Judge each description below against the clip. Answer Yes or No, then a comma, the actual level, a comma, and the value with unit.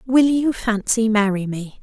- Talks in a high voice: Yes, high, 225 Hz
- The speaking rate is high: No, average, 165 wpm